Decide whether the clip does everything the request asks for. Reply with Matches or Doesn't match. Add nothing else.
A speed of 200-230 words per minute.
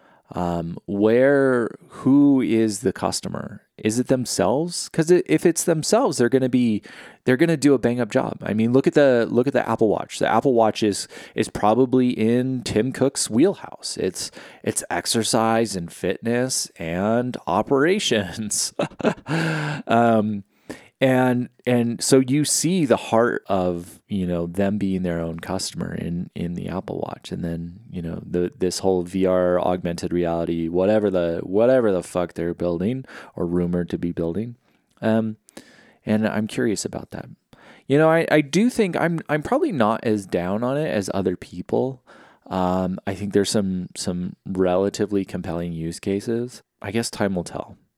Doesn't match